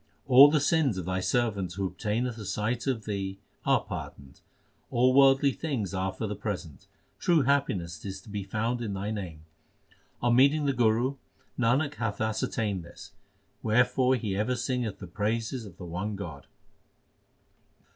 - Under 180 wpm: Yes, average, 160 wpm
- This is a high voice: No, low, 110 Hz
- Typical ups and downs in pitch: Yes, average, 4.6 semitones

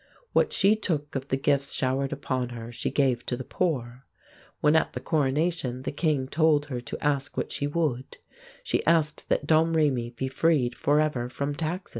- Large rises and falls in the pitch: No, average, 3.3 semitones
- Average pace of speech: Yes, average, 180 wpm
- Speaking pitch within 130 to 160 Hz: Yes, medium, 140 Hz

